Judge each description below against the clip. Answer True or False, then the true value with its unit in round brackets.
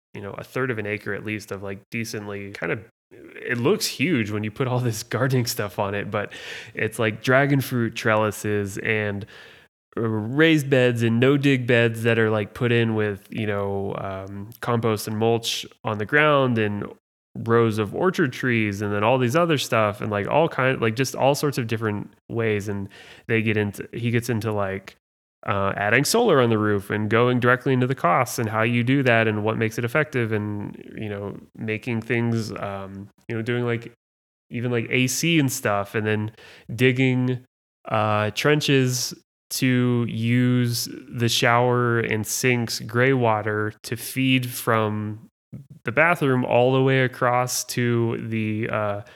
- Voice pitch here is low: True (115 Hz)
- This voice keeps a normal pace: True (180 wpm)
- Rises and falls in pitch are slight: False (3.0 semitones)